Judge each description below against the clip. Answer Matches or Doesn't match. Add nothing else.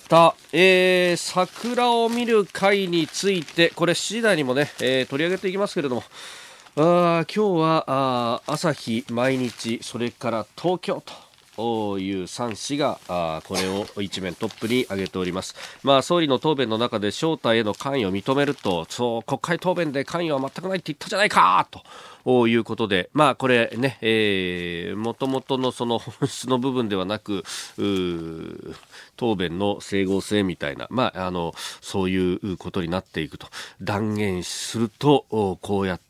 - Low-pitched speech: Matches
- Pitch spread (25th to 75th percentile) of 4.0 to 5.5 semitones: Doesn't match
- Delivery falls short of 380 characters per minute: Matches